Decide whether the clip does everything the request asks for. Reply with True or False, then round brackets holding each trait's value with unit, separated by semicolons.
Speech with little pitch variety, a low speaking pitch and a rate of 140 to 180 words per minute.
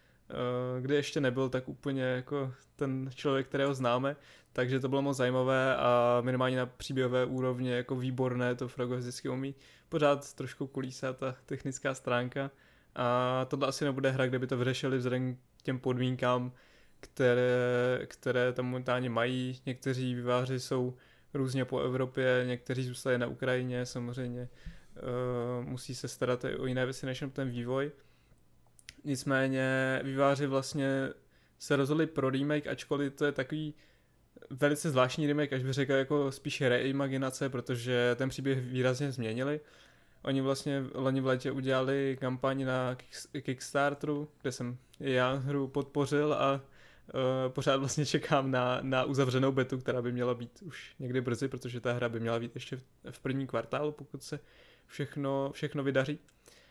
True (1.6 semitones; 130 Hz; 150 wpm)